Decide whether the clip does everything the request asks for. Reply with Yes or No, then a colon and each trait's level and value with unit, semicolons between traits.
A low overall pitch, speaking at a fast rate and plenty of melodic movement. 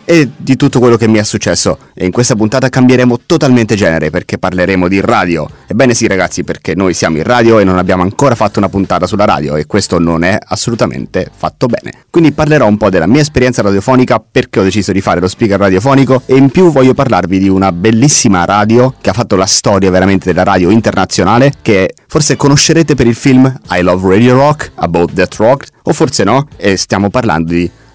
Yes: low, 110 Hz; fast, 210 wpm; wide, 5.7 semitones